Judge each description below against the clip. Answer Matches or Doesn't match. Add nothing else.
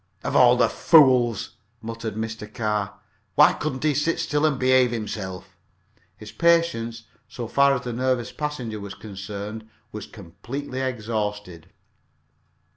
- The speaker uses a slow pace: Matches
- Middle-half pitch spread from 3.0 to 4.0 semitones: Matches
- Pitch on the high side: Doesn't match